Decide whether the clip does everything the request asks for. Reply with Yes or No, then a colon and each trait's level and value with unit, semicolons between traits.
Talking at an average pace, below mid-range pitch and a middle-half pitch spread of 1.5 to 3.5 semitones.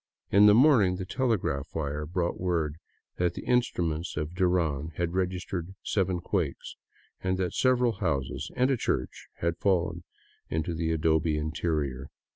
Yes: average, 150 wpm; very low, 85 Hz; average, 3.2 semitones